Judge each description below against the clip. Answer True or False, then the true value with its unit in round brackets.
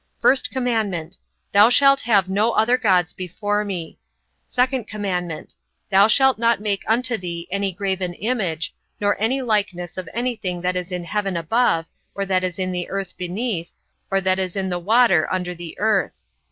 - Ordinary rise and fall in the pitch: True (3.8 semitones)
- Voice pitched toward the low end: False (195 Hz)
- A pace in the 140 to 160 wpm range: False (175 wpm)